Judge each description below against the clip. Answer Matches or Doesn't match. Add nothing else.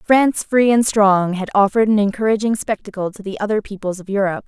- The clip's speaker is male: Doesn't match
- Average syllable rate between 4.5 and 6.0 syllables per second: Doesn't match